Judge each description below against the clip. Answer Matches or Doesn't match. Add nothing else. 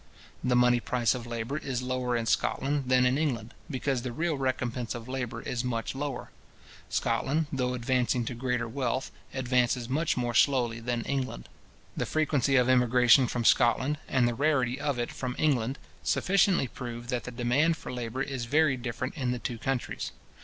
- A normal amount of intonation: Doesn't match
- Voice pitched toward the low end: Matches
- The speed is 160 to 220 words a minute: Matches